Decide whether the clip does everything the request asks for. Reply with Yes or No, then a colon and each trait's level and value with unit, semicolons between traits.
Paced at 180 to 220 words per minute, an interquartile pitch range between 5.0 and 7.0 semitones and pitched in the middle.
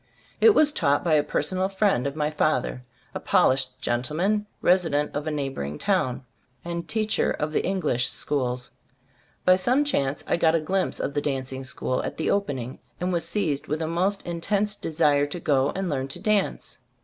Yes: average, 185 wpm; wide, 5.4 semitones; medium, 155 Hz